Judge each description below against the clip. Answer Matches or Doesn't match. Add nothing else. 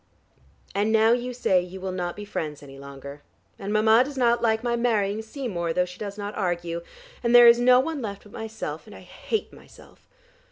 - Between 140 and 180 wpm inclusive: Doesn't match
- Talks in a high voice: Matches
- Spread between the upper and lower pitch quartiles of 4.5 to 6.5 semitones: Matches